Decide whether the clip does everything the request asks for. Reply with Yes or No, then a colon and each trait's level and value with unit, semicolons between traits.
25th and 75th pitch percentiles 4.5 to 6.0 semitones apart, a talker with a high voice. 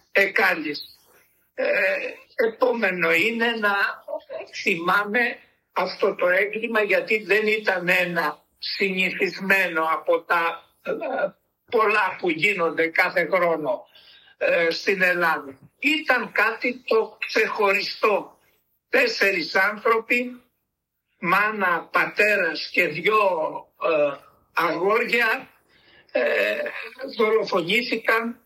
Yes: average, 5.1 semitones; high, 215 Hz